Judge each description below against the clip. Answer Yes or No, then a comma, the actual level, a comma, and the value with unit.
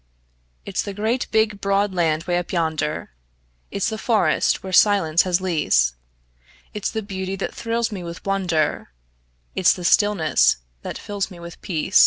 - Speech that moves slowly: No, average, 160 wpm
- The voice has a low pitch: No, high, 190 Hz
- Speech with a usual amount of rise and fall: Yes, average, 3.3 semitones